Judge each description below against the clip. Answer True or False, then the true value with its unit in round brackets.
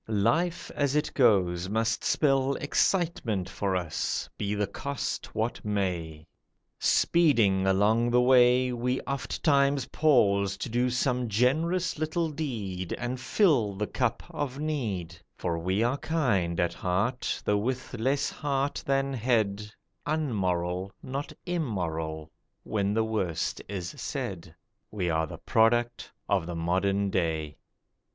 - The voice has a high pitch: False (110 Hz)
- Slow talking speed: True (130 wpm)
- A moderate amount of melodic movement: False (6.2 semitones)